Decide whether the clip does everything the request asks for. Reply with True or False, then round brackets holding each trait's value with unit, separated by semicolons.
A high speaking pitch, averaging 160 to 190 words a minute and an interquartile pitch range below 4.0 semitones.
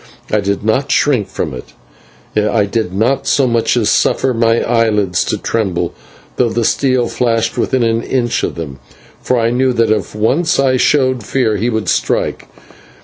False (115 Hz; 175 wpm; 3.2 semitones)